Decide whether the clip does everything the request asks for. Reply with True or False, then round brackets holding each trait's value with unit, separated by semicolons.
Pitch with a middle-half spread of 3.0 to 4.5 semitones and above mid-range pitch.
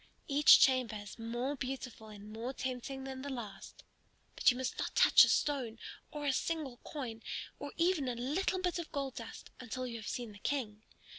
True (3.6 semitones; 255 Hz)